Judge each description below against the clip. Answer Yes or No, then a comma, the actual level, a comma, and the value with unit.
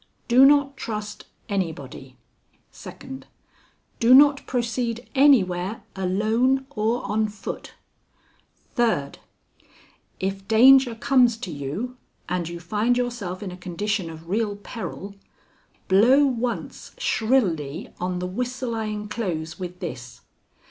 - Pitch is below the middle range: No, high, 215 Hz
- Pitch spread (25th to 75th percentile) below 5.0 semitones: No, average, 5.3 semitones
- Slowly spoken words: Yes, slow, 115 wpm